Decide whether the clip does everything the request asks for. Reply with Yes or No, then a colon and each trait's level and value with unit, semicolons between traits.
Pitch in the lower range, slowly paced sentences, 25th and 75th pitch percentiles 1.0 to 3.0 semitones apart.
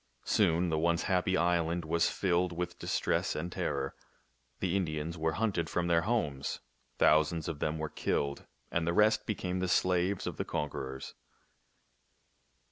No: very low, 85 Hz; average, 150 wpm; narrow, 2.6 semitones